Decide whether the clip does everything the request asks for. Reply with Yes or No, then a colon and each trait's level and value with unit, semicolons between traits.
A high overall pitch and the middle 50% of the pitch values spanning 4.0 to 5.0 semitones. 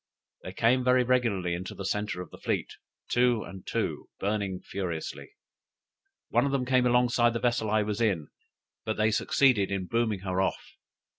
No: low, 110 Hz; average, 4.3 semitones